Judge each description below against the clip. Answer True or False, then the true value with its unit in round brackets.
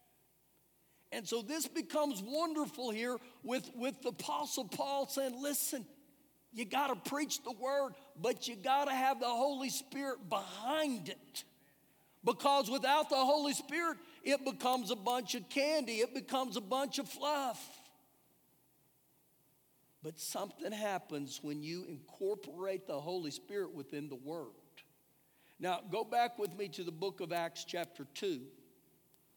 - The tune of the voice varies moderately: False (6.3 semitones)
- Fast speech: False (140 wpm)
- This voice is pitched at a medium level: False (255 Hz)